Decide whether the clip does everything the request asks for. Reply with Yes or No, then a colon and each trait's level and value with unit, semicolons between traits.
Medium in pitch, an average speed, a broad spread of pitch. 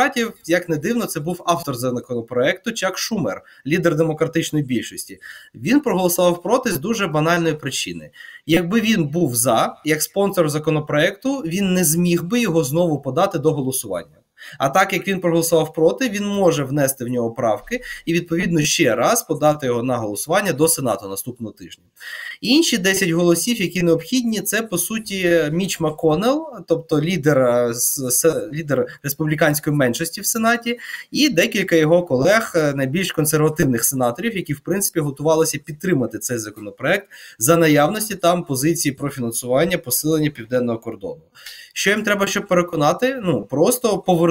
No: medium, 165 Hz; average, 145 wpm; average, 4.7 semitones